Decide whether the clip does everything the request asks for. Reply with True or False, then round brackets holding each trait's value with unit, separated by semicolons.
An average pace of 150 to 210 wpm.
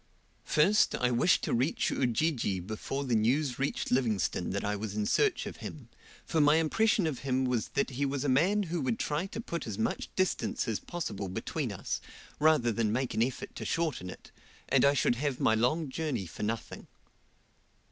True (195 wpm)